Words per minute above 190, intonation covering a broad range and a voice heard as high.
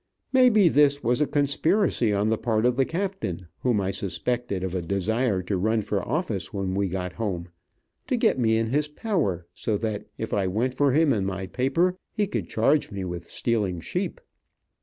No: average, 200 wpm; wide, 6.7 semitones; low, 110 Hz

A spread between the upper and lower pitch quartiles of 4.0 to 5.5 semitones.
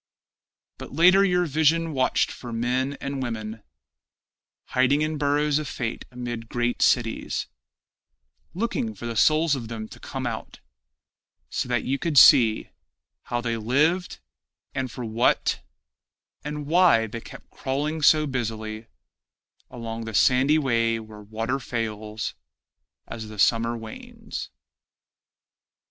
Yes: average, 4.7 semitones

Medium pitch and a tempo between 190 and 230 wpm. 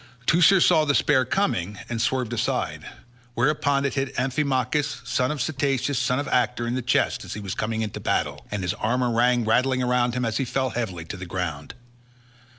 No: low, 125 Hz; average, 195 wpm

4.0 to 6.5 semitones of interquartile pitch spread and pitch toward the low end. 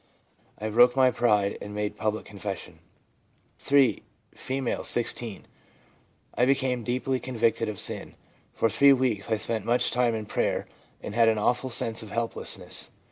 No: average, 2.8 semitones; low, 115 Hz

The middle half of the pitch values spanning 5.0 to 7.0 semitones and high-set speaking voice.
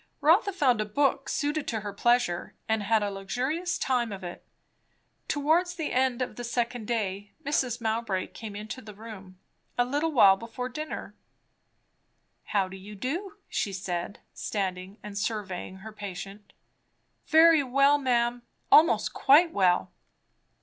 Yes: wide, 5.5 semitones; high, 230 Hz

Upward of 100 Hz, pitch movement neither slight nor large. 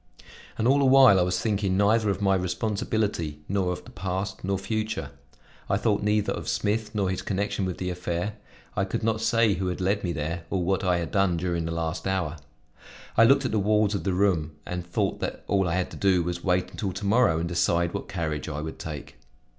No: very low, 95 Hz; average, 3.1 semitones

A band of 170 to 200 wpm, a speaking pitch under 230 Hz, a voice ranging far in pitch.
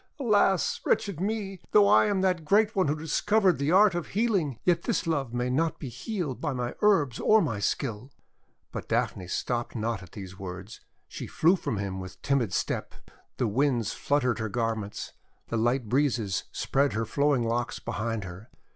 Yes: average, 180 wpm; low, 135 Hz; wide, 8.1 semitones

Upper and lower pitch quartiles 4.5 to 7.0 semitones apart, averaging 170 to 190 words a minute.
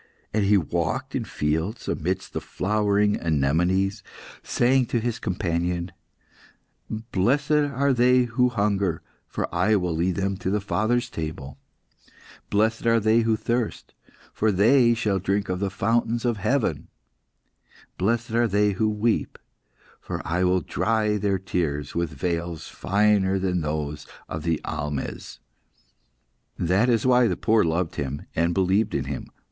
No: average, 4.8 semitones; average, 145 wpm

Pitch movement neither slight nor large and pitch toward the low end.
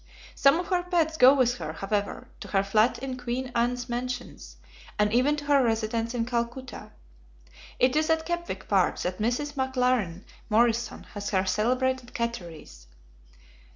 No: average, 3.6 semitones; high, 245 Hz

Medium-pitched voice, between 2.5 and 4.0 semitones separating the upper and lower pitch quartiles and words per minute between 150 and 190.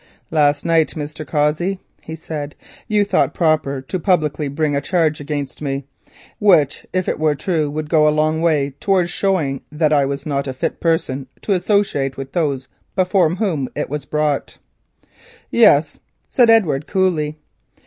Yes: medium, 155 Hz; average, 3.5 semitones; average, 160 wpm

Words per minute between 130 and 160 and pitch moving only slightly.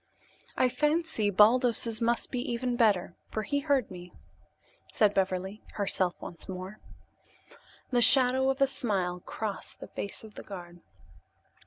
No: average, 140 wpm; average, 4.9 semitones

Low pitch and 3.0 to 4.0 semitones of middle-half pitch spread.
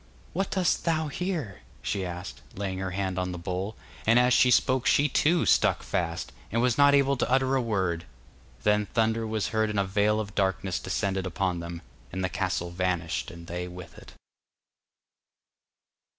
No: low, 100 Hz; average, 5.2 semitones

